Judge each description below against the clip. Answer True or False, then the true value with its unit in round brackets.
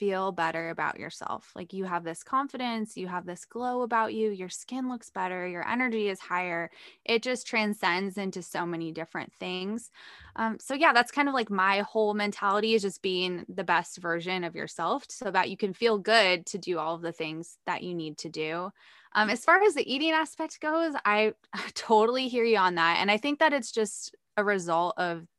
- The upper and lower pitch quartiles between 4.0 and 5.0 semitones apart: True (4.7 semitones)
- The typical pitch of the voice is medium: False (200 Hz)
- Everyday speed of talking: False (210 wpm)